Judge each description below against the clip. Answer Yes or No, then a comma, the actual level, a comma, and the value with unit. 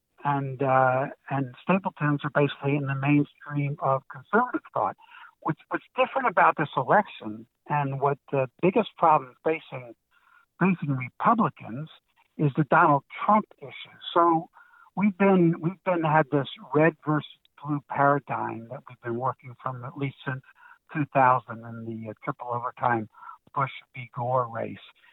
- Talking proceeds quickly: No, average, 140 wpm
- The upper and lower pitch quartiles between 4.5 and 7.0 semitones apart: Yes, average, 4.9 semitones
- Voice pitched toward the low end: No, medium, 145 Hz